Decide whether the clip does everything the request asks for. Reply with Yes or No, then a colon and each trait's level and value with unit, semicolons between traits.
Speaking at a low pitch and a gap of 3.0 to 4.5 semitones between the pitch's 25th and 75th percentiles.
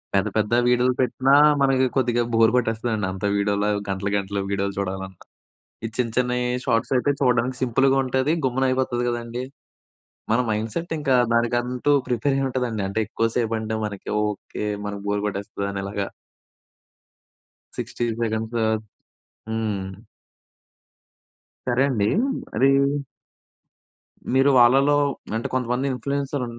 Yes: low, 120 Hz; average, 3.5 semitones